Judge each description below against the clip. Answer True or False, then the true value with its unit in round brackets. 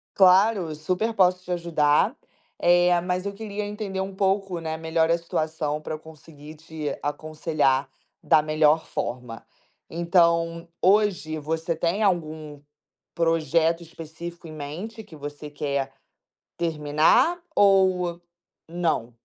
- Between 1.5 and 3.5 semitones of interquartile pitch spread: True (2.9 semitones)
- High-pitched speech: False (165 Hz)